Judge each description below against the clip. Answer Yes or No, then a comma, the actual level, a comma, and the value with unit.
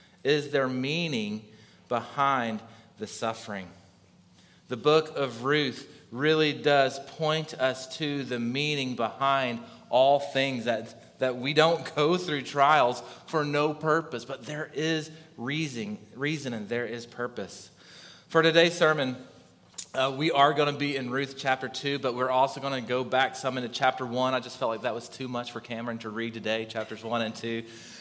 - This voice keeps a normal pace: Yes, average, 170 wpm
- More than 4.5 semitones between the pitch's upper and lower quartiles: No, average, 3.8 semitones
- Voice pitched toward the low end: Yes, low, 130 Hz